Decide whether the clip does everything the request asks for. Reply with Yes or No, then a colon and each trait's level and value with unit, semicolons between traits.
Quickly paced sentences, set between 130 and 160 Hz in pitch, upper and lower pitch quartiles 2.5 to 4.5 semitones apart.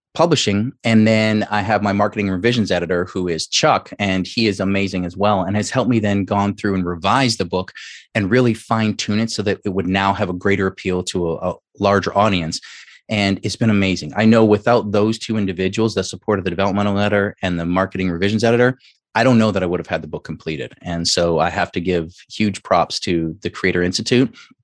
No: fast, 220 wpm; low, 100 Hz; average, 2.9 semitones